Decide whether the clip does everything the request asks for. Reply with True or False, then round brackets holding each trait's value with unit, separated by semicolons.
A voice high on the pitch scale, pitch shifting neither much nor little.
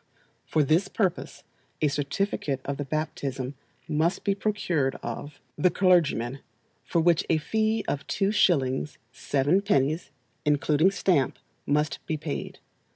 False (155 Hz; 4.6 semitones)